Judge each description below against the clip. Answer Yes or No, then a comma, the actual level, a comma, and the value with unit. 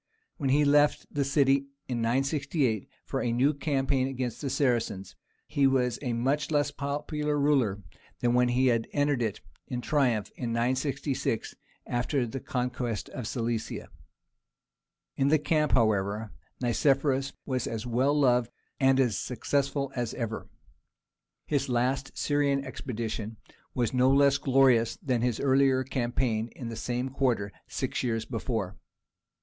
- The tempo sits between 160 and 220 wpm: No, average, 140 wpm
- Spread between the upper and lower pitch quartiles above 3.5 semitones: No, average, 2.9 semitones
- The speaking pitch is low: Yes, low, 130 Hz